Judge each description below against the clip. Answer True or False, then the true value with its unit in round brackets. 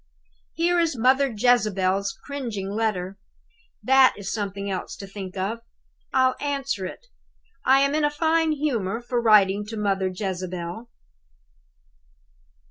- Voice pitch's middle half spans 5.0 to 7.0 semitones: True (5.6 semitones)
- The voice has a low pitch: False (220 Hz)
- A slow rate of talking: True (130 wpm)